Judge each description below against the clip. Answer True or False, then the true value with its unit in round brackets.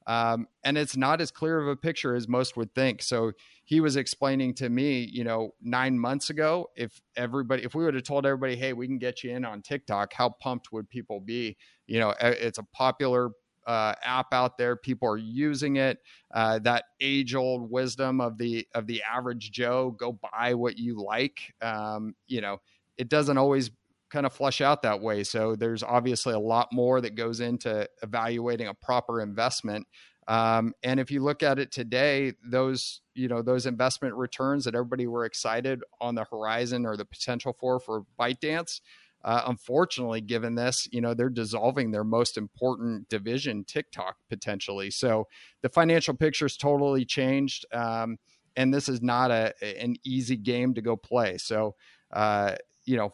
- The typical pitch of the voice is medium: False (125 Hz)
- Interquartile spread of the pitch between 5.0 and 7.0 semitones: False (2.5 semitones)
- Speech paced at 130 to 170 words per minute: False (185 wpm)